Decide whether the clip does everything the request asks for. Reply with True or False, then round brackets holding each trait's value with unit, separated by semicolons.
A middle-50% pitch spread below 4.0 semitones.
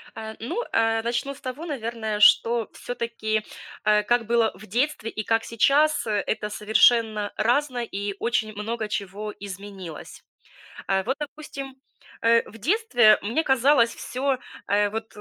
True (3.0 semitones)